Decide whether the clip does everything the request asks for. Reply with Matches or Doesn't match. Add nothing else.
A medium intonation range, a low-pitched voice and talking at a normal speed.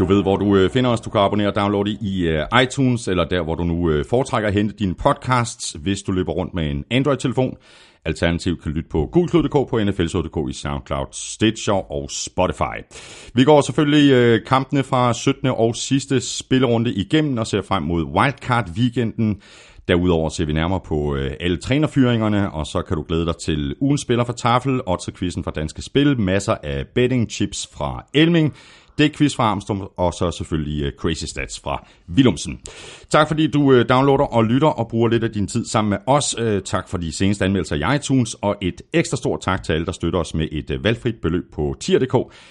Doesn't match